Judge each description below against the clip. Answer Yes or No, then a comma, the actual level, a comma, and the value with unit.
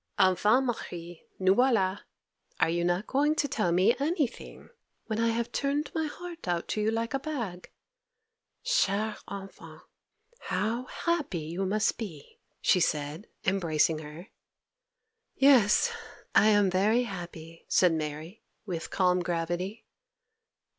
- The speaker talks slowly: Yes, slow, 130 wpm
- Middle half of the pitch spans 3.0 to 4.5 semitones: No, wide, 5.6 semitones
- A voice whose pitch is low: No, high, 200 Hz